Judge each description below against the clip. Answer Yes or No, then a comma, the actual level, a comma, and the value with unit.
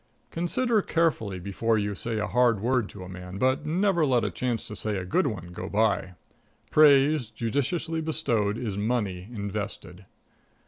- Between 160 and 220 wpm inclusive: Yes, average, 165 wpm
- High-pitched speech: No, low, 115 Hz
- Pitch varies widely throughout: Yes, wide, 5.9 semitones